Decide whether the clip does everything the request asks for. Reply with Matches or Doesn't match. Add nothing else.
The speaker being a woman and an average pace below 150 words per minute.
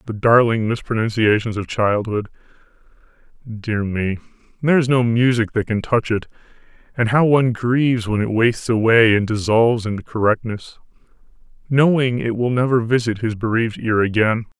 Doesn't match